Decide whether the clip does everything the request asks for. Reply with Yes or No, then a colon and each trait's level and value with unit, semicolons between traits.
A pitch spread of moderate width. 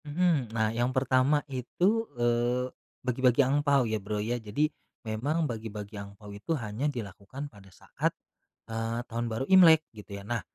Yes: average, 4.5 semitones